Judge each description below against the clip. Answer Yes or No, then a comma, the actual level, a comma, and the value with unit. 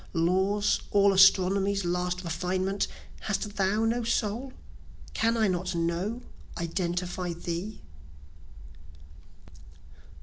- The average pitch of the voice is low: No, high, 190 Hz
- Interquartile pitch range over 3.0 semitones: No, narrow, 2.6 semitones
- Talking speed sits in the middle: No, slow, 90 wpm